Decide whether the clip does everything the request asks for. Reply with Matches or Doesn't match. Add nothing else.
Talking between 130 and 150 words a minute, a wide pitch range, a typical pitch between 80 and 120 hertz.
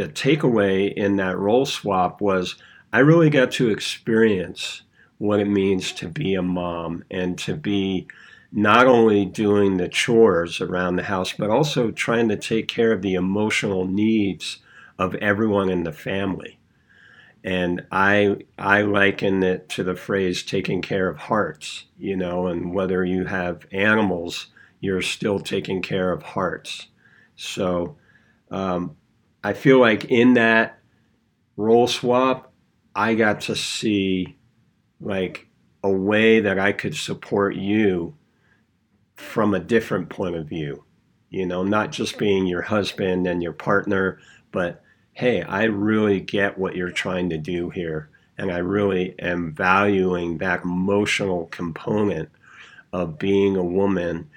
Doesn't match